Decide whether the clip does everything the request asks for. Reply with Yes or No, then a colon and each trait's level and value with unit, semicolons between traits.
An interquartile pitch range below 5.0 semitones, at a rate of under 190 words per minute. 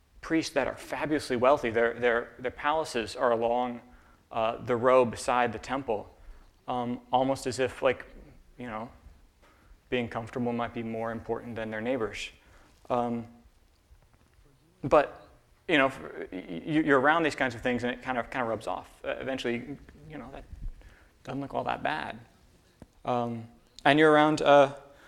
Yes: narrow, 2.4 semitones; average, 160 wpm